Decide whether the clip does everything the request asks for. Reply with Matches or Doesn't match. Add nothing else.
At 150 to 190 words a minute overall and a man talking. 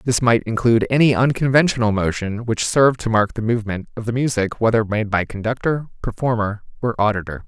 Matches